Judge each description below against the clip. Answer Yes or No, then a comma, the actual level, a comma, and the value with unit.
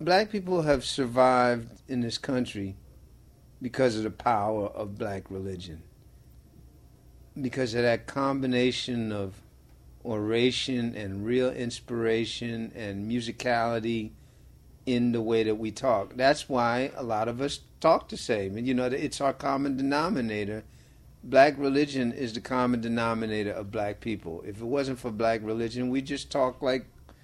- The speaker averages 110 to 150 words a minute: Yes, average, 145 wpm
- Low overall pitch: Yes, low, 120 Hz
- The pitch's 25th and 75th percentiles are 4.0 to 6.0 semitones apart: No, average, 3.1 semitones